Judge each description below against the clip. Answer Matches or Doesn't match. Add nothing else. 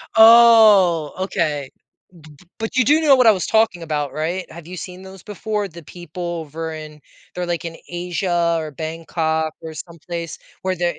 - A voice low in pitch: Doesn't match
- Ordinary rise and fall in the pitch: Matches